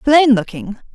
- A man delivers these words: No, female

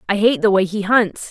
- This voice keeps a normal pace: No, fast, 275 wpm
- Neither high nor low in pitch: No, high, 205 Hz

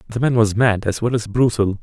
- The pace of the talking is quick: Yes, fast, 265 wpm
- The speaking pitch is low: Yes, low, 110 Hz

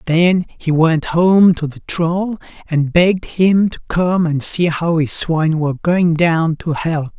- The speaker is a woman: No, male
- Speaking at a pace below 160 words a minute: No, average, 185 wpm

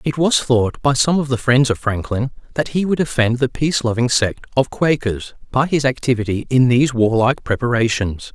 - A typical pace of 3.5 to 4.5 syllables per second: No, 5.3 syllables/s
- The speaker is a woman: No, male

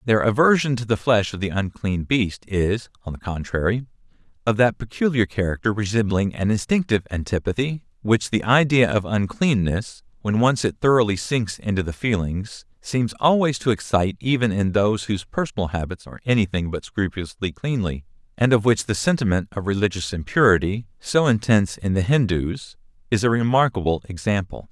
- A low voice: Yes, low, 105 Hz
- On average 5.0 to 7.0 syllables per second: Yes, 5.4 syllables/s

